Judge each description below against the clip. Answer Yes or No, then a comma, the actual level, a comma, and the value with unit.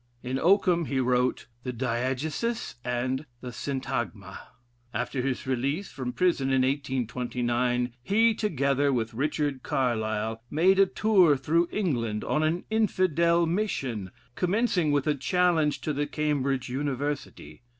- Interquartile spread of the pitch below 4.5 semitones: No, average, 5.2 semitones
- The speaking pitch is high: No, medium, 140 Hz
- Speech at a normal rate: No, slow, 125 wpm